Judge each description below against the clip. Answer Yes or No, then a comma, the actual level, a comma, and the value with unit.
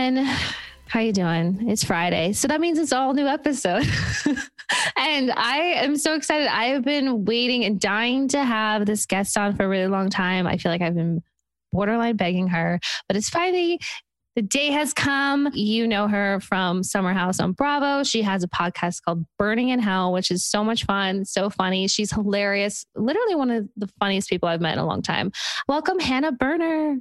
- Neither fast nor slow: Yes, average, 195 wpm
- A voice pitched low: No, high, 210 Hz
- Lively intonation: Yes, wide, 6.5 semitones